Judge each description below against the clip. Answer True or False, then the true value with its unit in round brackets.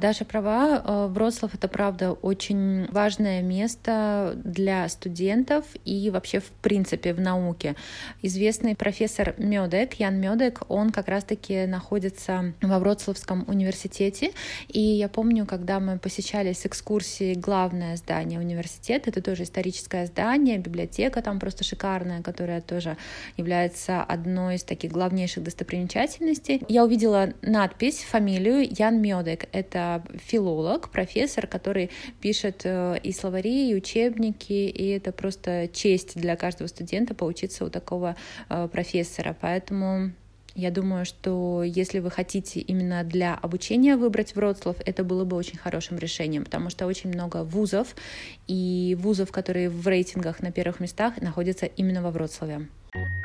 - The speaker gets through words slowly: False (130 wpm)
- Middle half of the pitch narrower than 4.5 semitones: True (2.8 semitones)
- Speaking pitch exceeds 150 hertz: True (190 Hz)